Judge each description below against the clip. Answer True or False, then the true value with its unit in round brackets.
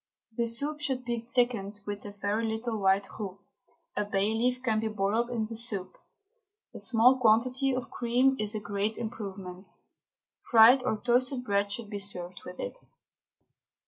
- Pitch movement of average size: True (3.3 semitones)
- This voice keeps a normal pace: True (165 wpm)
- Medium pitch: False (220 Hz)